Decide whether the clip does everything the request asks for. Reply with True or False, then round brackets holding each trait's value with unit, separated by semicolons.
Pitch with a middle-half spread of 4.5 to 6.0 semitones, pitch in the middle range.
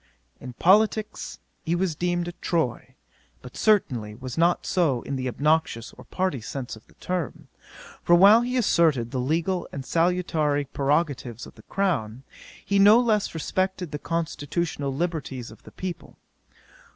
True (5.4 semitones; 165 Hz)